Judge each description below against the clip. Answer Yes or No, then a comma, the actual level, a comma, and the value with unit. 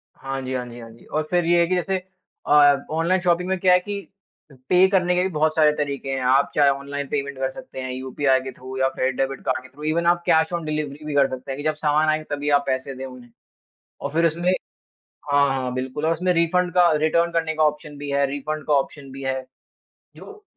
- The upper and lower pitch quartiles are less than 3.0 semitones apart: No, average, 3.9 semitones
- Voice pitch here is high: No, medium, 145 Hz